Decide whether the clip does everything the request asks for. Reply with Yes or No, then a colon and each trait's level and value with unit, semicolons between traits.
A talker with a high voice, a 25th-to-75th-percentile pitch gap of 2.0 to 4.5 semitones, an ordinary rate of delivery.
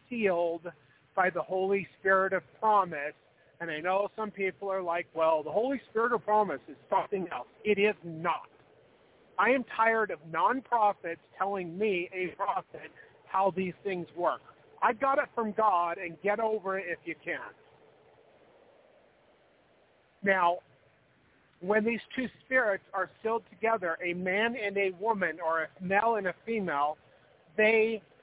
Yes: high, 195 Hz; average, 4.2 semitones; average, 150 wpm